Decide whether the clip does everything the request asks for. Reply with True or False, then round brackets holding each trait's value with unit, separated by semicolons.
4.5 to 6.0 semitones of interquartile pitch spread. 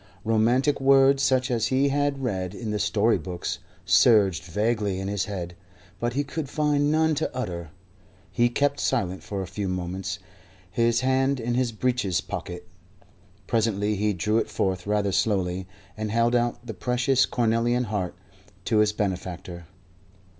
True (4.9 semitones)